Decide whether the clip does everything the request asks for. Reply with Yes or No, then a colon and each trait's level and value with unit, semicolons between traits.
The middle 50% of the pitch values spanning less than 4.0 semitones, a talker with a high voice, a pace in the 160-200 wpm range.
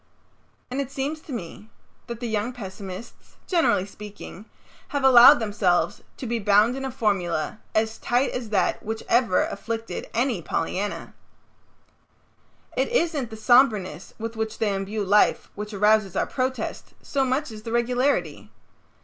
No: average, 3.6 semitones; high, 225 Hz; average, 150 wpm